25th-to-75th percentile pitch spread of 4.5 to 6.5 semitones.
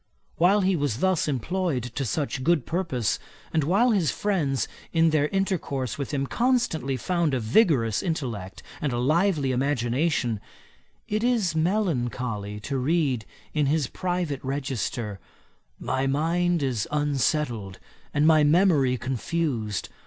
Yes: wide, 5.4 semitones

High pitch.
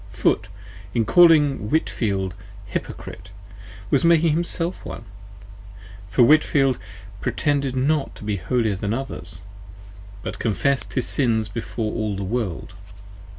No: low, 120 Hz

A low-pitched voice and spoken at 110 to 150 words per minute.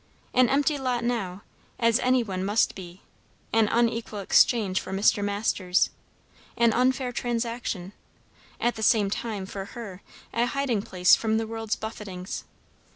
No: high, 225 Hz; average, 145 wpm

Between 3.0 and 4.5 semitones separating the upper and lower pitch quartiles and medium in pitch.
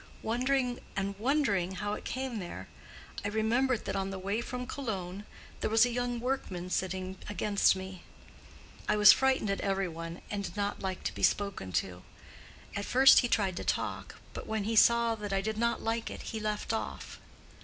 No: average, 3.4 semitones; high, 210 Hz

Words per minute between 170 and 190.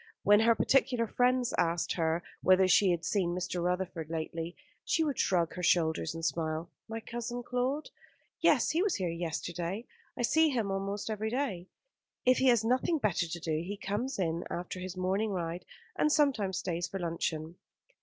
Yes: average, 175 wpm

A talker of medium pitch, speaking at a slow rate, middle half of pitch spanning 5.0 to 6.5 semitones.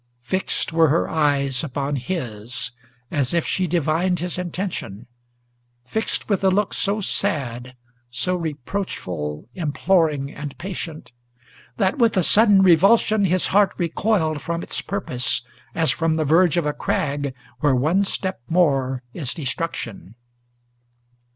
Yes: medium, 160 Hz; slow, 130 wpm; wide, 5.4 semitones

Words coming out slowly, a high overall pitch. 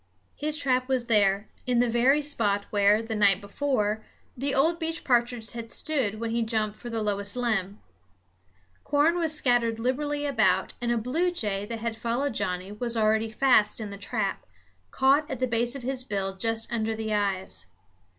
No: average, 180 wpm; high, 230 Hz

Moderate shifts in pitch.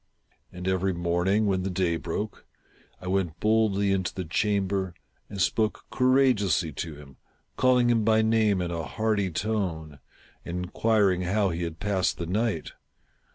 Yes: average, 3.6 semitones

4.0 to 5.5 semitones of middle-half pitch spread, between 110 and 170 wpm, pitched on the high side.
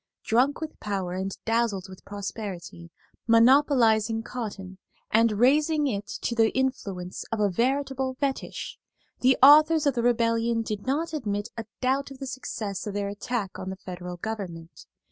Yes: average, 4.8 semitones; average, 155 wpm; high, 225 Hz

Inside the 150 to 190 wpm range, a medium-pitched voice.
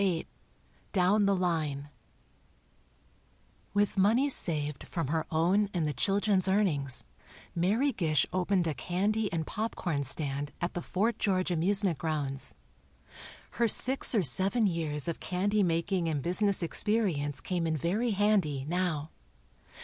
No: slow, 135 wpm; medium, 180 Hz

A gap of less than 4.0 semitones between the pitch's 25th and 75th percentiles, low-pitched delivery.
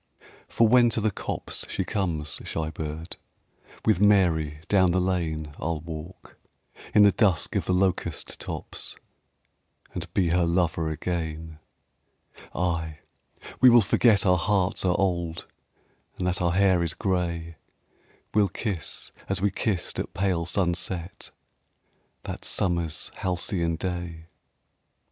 Yes: average, 2.7 semitones; very low, 90 Hz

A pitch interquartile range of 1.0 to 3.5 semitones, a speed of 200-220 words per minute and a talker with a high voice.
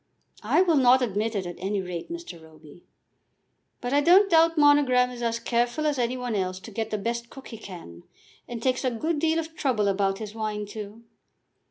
No: wide, 5.5 semitones; fast, 205 wpm; high, 235 Hz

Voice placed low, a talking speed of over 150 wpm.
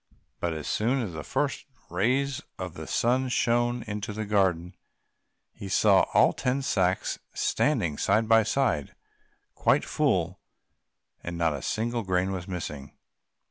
No: low, 105 Hz; average, 145 wpm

